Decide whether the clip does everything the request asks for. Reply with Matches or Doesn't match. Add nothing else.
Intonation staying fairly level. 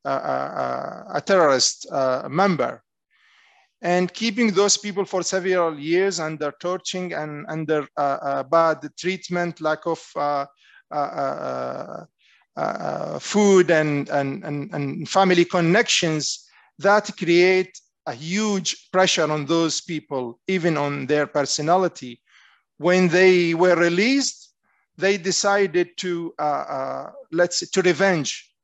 Doesn't match